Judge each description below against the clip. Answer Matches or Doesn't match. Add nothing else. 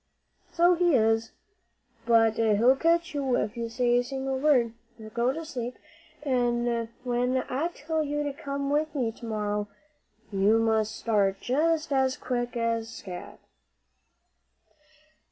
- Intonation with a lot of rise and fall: Doesn't match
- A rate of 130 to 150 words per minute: Matches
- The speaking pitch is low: Doesn't match